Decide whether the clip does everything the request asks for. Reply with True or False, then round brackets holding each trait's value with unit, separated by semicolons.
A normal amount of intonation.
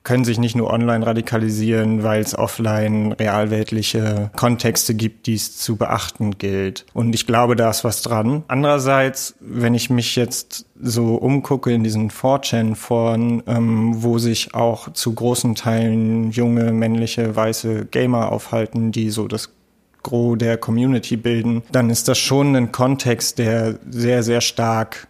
False (1.3 semitones)